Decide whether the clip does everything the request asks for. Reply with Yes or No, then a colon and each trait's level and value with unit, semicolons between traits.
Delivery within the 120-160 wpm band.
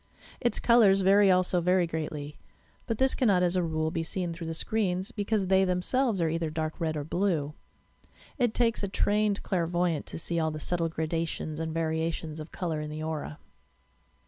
No: average, 185 wpm